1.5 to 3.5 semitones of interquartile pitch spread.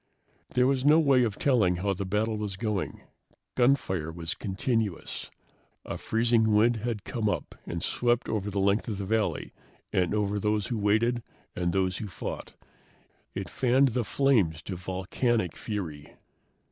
No: average, 4.0 semitones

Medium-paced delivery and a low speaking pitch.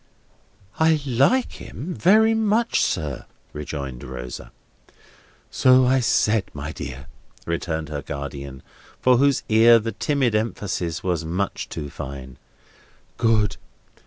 No: slow, 115 wpm; low, 100 Hz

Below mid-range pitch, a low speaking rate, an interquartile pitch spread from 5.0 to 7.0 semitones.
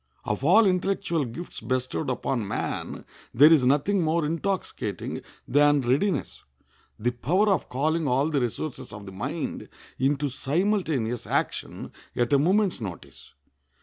No: medium, 145 Hz; slow, 130 wpm; wide, 5.5 semitones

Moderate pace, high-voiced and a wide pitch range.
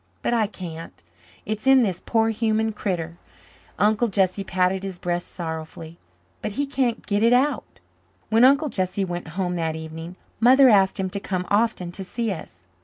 No: average, 175 wpm; high, 195 Hz; average, 4.3 semitones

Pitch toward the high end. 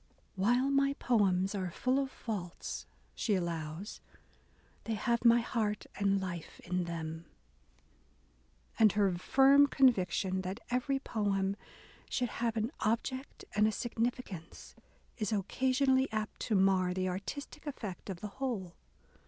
Yes: high, 210 Hz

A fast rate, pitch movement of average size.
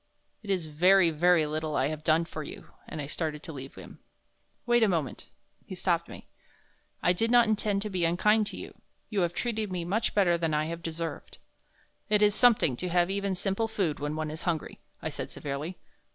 Yes: fast, 210 wpm; average, 4.4 semitones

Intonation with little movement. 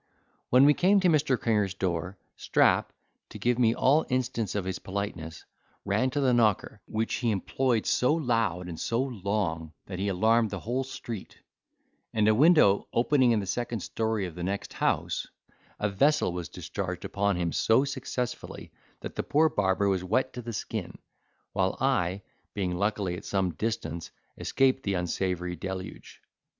No: average, 5.0 semitones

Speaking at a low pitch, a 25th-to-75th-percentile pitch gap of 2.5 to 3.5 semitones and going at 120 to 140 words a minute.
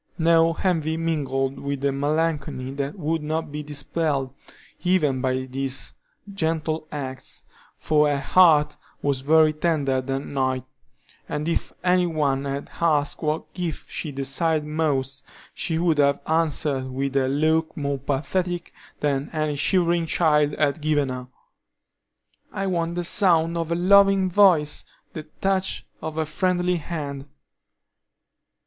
No: medium, 155 Hz; average, 3.0 semitones; slow, 135 wpm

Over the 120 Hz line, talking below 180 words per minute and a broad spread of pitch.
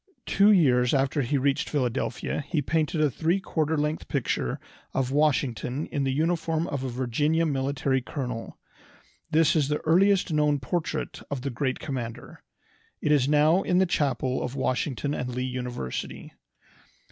No: medium, 140 Hz; average, 155 wpm; average, 3.4 semitones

